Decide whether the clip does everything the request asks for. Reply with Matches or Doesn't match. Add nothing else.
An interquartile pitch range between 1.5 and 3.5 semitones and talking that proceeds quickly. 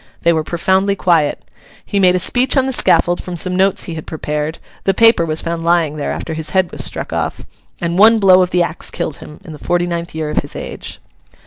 Matches